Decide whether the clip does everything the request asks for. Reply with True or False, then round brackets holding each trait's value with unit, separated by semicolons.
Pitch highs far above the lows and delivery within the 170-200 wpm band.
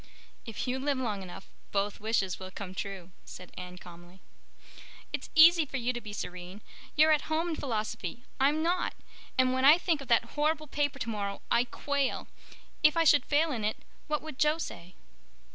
True (7.2 semitones; 180 wpm)